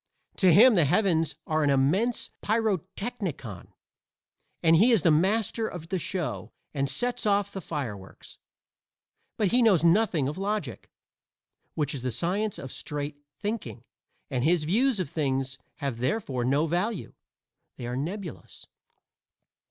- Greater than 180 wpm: No, average, 140 wpm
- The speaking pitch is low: No, medium, 170 Hz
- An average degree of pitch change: No, wide, 6.7 semitones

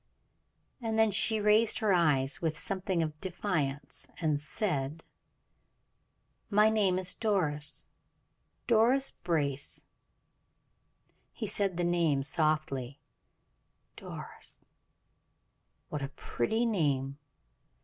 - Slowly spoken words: Yes, slow, 95 wpm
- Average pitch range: No, wide, 6.2 semitones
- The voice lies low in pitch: No, medium, 170 Hz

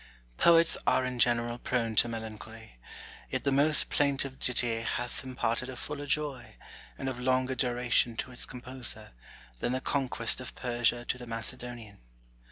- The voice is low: Yes, low, 125 Hz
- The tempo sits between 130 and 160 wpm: Yes, average, 155 wpm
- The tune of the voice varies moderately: No, narrow, 1.9 semitones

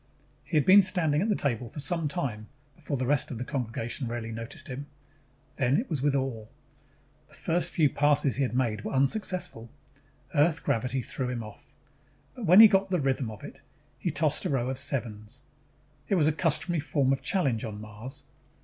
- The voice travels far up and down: No, average, 4.8 semitones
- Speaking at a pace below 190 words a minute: No, average, 195 wpm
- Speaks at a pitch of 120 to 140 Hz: Yes, low, 135 Hz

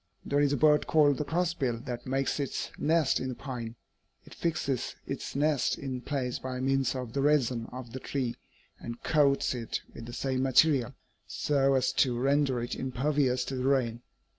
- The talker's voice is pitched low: Yes, low, 130 Hz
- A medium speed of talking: Yes, average, 185 wpm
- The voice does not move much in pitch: Yes, narrow, 2.3 semitones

